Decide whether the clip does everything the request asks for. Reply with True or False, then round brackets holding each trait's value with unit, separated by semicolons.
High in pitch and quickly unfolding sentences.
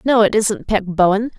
True (210 Hz; 215 wpm)